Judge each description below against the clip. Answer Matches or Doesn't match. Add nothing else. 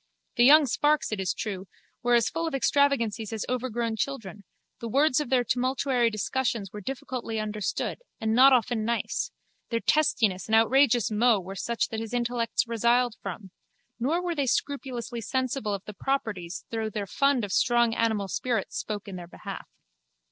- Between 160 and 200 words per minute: Matches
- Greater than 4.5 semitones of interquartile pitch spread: Doesn't match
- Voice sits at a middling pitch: Doesn't match